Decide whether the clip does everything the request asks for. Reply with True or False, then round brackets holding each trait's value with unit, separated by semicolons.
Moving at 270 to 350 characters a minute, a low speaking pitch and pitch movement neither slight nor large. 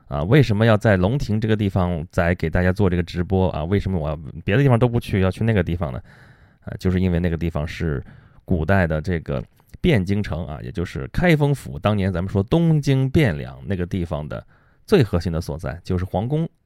True (320 characters per minute; 95 Hz; 4.2 semitones)